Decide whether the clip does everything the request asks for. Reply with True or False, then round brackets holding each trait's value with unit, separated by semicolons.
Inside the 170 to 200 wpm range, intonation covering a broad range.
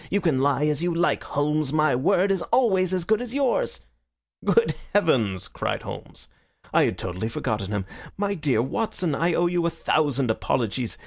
True (180 wpm; 6.3 semitones)